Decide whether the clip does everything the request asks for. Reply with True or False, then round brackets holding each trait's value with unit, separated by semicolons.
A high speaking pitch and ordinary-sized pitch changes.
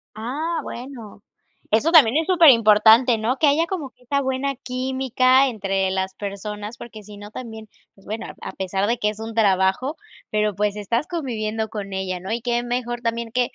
True (230 Hz; 3.7 semitones)